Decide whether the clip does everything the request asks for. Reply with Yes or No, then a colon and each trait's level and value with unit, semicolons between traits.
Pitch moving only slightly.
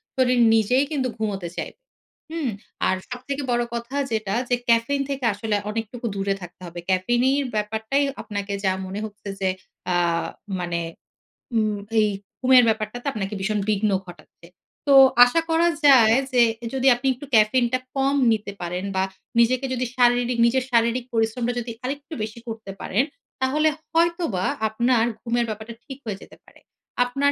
No: average, 3.5 semitones